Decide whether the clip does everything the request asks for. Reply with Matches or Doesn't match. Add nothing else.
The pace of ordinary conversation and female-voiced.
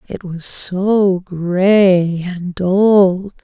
Doesn't match